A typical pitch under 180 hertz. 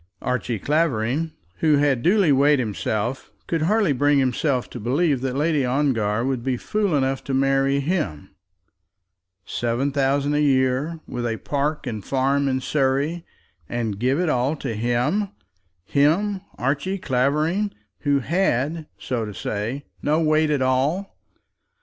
Yes: medium, 140 Hz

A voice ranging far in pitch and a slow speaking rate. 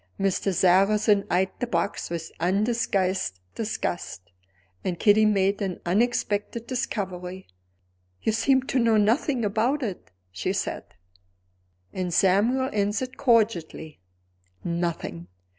No: average, 4.1 semitones; slow, 110 wpm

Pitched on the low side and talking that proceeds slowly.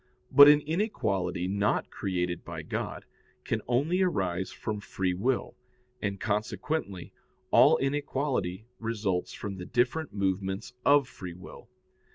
Yes: low, 105 Hz; slow, 125 wpm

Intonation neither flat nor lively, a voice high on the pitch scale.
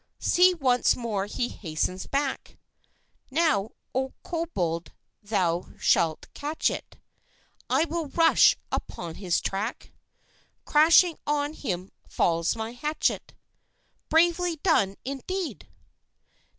No: wide, 8.8 semitones; very high, 265 Hz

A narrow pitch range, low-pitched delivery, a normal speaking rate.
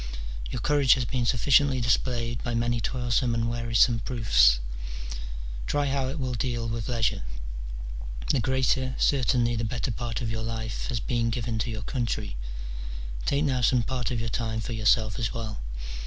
Yes: narrow, 2.1 semitones; low, 120 Hz; average, 170 wpm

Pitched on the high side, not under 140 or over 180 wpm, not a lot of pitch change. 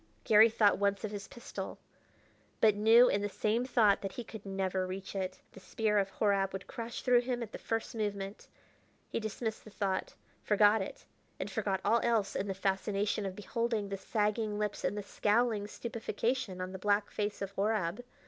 No: high, 210 Hz; average, 190 wpm; narrow, 2.3 semitones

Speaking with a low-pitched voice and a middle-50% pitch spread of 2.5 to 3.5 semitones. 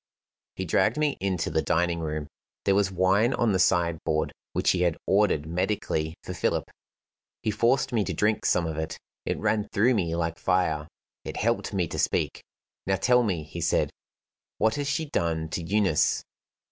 No: very low, 95 Hz; average, 4.6 semitones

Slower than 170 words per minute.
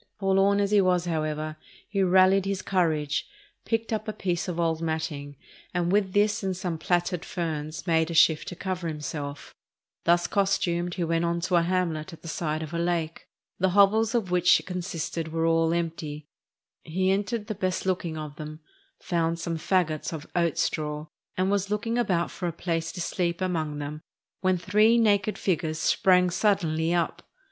No: average, 180 wpm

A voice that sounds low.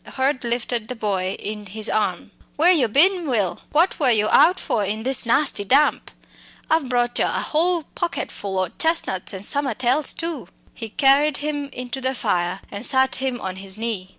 No: very high, 250 Hz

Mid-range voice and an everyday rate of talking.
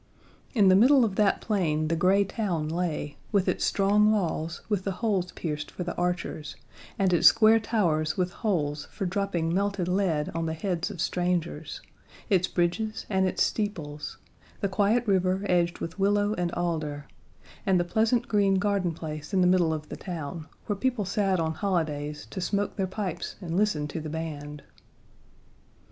Yes: medium, 180 Hz; average, 175 wpm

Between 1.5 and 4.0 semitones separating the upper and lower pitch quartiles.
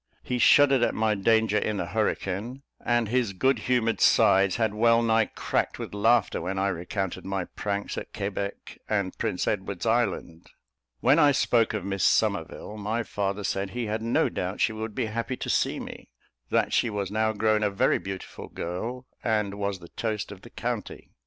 Yes: average, 2.9 semitones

